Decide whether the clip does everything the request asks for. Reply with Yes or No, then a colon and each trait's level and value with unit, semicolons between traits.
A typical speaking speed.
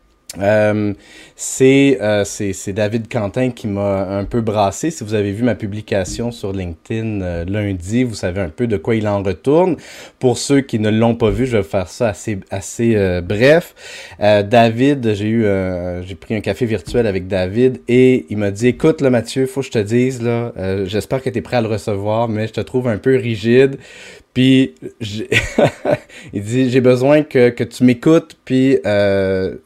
Yes: average, 200 wpm